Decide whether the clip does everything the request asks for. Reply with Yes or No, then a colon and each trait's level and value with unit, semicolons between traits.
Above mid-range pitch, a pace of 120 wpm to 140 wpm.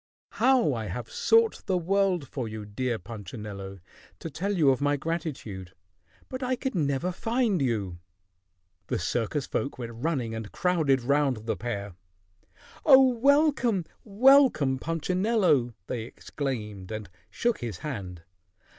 No: medium, 140 Hz; slow, 135 wpm